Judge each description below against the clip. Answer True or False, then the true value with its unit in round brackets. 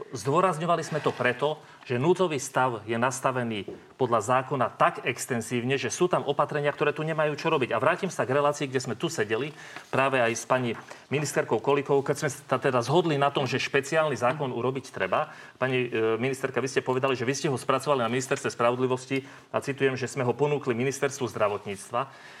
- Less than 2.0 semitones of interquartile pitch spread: False (2.6 semitones)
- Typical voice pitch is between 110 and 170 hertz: True (135 Hz)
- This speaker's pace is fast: True (185 wpm)